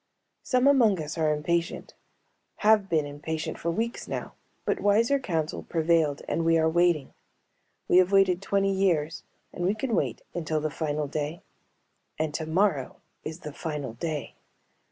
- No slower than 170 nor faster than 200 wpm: No, average, 155 wpm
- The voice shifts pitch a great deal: No, average, 4.2 semitones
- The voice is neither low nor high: Yes, medium, 165 Hz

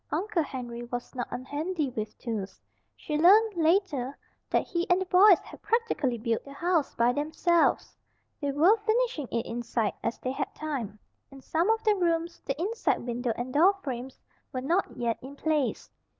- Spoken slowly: No, average, 175 wpm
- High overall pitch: Yes, very high, 295 Hz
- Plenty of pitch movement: Yes, wide, 6.5 semitones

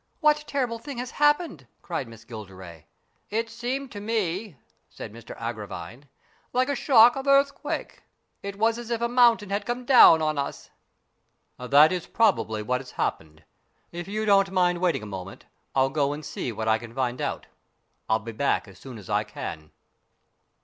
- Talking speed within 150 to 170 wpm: No, average, 185 wpm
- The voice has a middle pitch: Yes, medium, 170 Hz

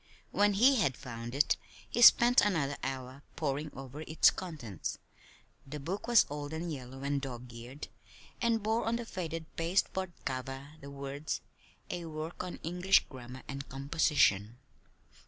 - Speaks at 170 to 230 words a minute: No, average, 150 wpm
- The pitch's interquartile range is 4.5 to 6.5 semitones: Yes, average, 5.1 semitones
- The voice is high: No, medium, 145 Hz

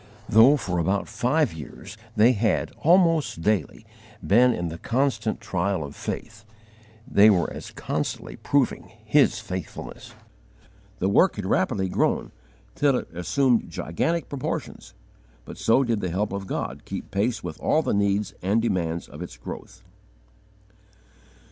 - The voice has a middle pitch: No, low, 105 Hz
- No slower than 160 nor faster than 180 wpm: No, average, 140 wpm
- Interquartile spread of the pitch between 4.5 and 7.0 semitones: Yes, wide, 5.4 semitones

